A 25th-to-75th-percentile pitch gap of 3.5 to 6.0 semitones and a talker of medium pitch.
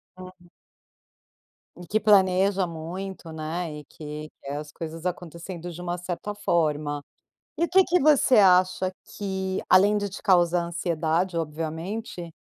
No: average, 2.8 semitones; medium, 175 Hz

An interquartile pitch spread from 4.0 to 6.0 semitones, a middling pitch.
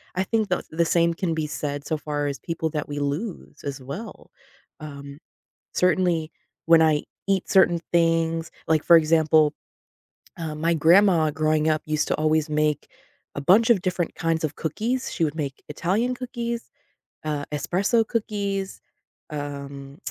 No: average, 3.5 semitones; medium, 160 Hz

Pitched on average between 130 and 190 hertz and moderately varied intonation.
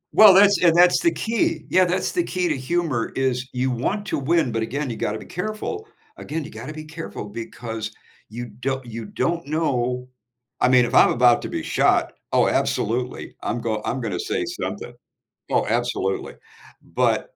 No: low, 135 Hz; wide, 6.7 semitones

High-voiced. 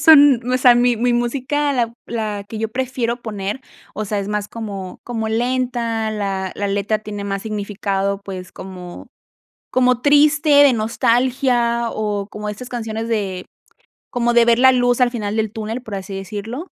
Yes: high, 225 Hz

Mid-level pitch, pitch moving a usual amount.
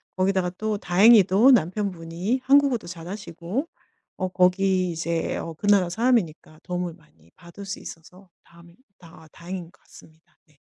Yes: medium, 180 Hz; average, 3.2 semitones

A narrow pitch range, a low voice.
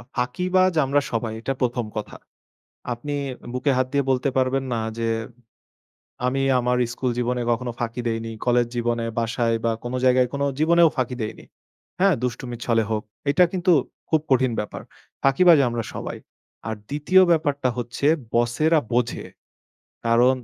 No: average, 3.3 semitones; low, 125 Hz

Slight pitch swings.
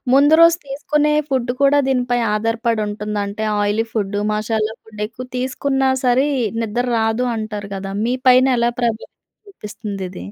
No: average, 3.6 semitones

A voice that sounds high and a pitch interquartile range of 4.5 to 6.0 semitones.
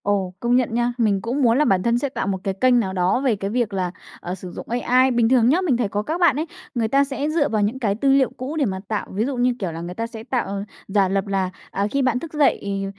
Yes: high, 230 Hz; average, 4.8 semitones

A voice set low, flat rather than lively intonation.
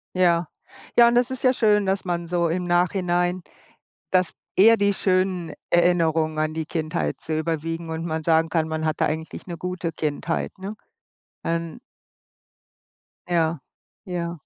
No: medium, 170 Hz; narrow, 2.3 semitones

